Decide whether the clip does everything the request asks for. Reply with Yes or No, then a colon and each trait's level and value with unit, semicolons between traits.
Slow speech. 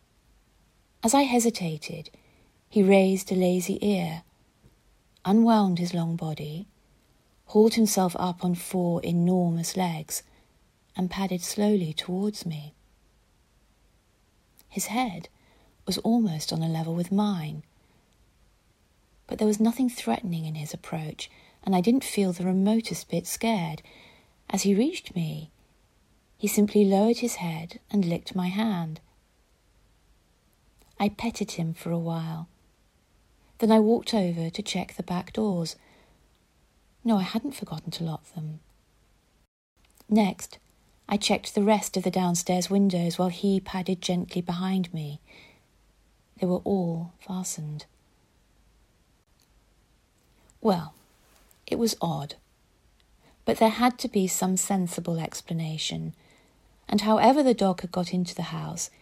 Yes: slow, 125 wpm